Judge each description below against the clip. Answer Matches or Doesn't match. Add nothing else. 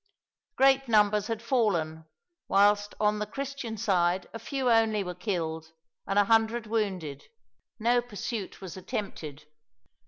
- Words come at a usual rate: Doesn't match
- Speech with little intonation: Doesn't match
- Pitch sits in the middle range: Doesn't match